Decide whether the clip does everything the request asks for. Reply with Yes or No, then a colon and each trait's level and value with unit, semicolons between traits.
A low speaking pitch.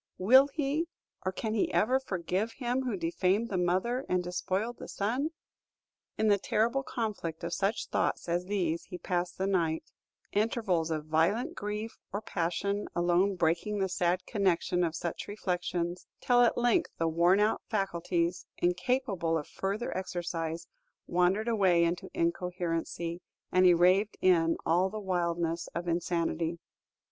No: medium, 185 Hz